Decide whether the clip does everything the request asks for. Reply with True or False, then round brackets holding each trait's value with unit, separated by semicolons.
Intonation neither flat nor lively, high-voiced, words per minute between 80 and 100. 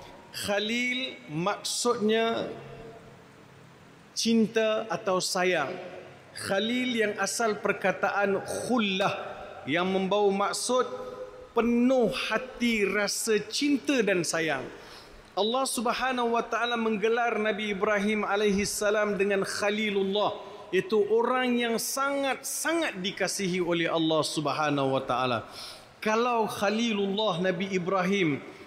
True (3.1 semitones; 205 Hz; 90 wpm)